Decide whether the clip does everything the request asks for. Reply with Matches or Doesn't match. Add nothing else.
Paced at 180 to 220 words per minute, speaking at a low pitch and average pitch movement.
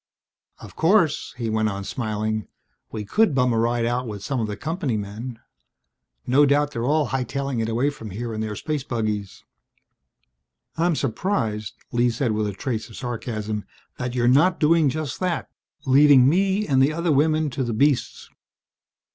Doesn't match